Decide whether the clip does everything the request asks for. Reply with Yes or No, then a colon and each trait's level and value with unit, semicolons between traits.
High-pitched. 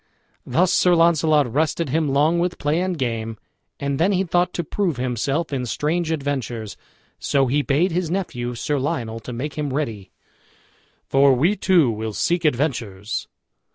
No: medium, 145 Hz